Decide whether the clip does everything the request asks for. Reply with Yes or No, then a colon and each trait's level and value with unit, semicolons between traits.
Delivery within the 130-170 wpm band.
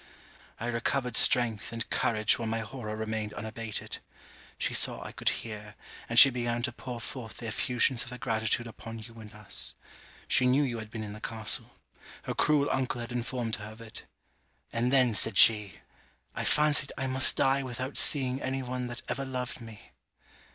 No: average, 185 wpm